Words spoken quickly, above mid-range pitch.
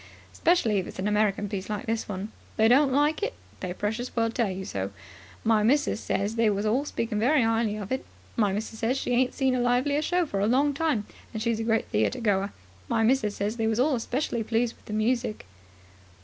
Yes: fast, 220 wpm; high, 225 Hz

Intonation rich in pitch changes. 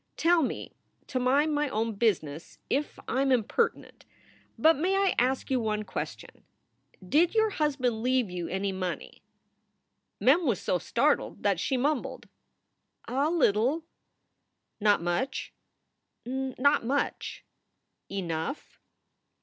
Yes: wide, 5.8 semitones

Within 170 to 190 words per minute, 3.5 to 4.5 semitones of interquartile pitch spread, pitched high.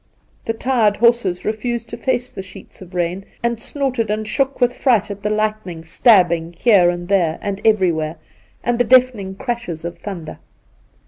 No: average, 175 wpm; average, 5.1 semitones; high, 210 Hz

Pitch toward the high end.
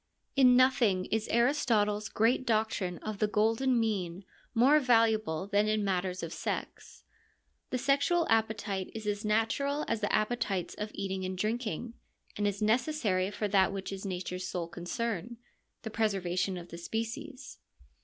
Yes: high, 215 Hz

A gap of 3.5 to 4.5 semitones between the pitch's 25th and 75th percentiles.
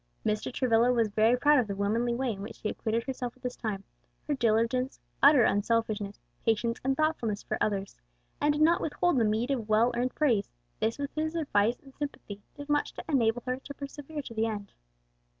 Yes: average, 4.2 semitones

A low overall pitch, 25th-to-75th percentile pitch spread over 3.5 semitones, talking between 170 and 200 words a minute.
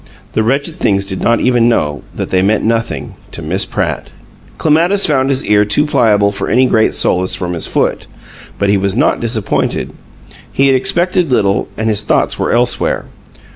Yes: low, 110 Hz; average, 4.8 semitones; average, 180 wpm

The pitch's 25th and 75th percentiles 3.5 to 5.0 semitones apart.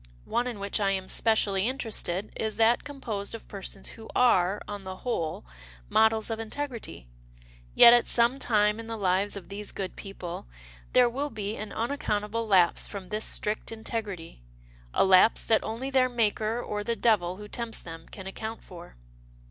No: average, 2.9 semitones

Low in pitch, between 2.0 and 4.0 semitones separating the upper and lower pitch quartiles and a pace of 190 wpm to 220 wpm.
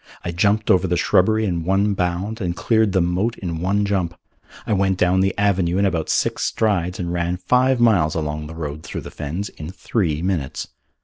Yes: very low, 90 Hz; average, 3.0 semitones; average, 200 wpm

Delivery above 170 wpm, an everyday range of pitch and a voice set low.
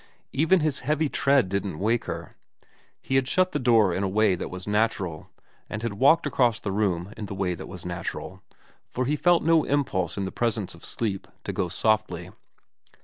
No: average, 200 wpm; wide, 6.1 semitones; low, 110 Hz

